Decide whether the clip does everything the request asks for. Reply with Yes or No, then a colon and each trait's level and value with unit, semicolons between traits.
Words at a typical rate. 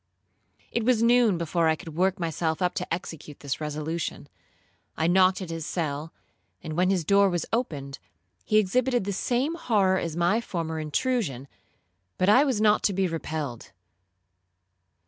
Yes: average, 165 wpm